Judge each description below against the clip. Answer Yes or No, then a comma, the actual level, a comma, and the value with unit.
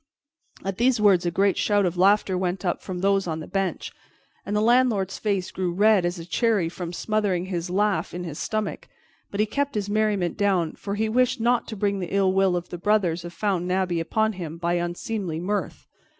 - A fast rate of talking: Yes, fast, 210 wpm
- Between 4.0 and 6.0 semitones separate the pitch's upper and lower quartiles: No, average, 3.0 semitones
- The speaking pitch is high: Yes, high, 195 Hz